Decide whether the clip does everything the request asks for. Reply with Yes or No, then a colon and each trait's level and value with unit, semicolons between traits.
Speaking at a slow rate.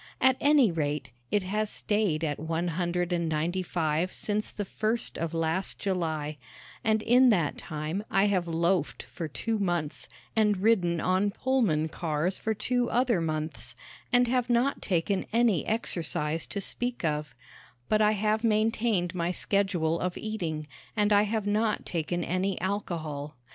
No: average, 155 wpm